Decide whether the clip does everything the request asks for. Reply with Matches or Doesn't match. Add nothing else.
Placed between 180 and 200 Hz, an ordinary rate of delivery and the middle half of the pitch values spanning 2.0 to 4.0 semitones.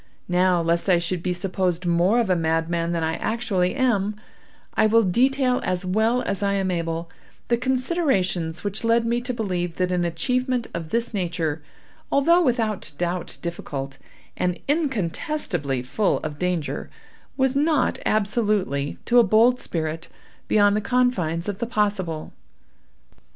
Doesn't match